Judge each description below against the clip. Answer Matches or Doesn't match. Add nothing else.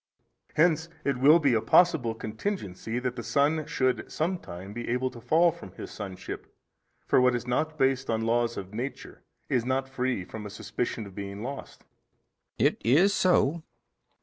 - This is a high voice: Doesn't match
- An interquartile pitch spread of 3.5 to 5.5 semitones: Matches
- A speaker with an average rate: Matches